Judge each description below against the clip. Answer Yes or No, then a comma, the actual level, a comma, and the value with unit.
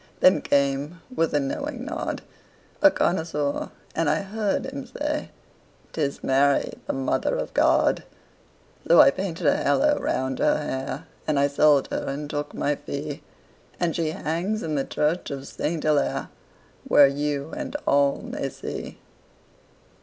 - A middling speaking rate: Yes, average, 150 wpm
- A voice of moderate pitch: Yes, medium, 150 Hz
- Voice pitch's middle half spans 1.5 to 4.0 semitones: No, average, 4.8 semitones